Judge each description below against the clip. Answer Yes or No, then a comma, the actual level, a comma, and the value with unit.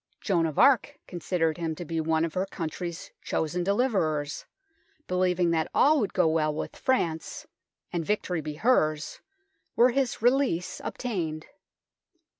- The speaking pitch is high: No, medium, 175 Hz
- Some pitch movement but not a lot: Yes, average, 4.6 semitones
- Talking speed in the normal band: Yes, average, 165 wpm